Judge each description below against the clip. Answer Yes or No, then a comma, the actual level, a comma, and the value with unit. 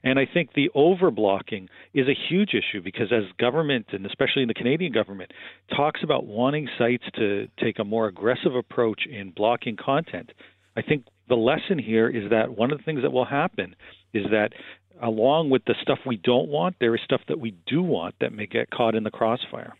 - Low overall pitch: Yes, low, 120 Hz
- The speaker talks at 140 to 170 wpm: No, fast, 205 wpm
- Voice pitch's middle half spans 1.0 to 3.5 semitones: No, average, 4.0 semitones